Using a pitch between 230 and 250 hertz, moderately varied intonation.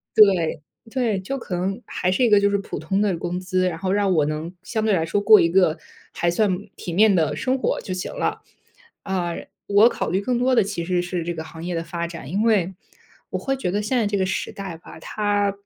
No: high, 190 Hz; average, 3.2 semitones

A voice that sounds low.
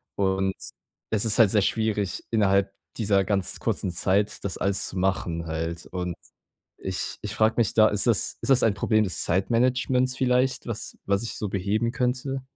Yes: low, 105 Hz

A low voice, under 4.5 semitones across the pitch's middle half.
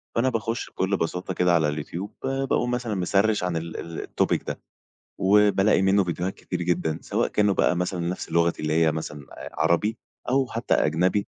Yes: very low, 90 Hz; average, 3.7 semitones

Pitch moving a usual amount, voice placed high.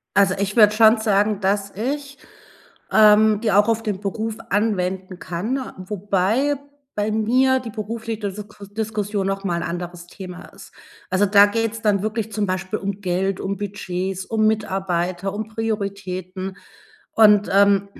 No: narrow, 2.3 semitones; high, 205 Hz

